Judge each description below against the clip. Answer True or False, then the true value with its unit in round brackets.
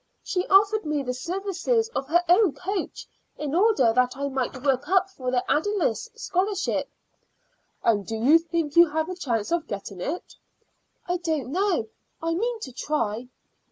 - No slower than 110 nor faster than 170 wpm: True (165 wpm)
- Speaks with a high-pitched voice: True (325 Hz)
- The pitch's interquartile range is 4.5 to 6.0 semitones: False (6.6 semitones)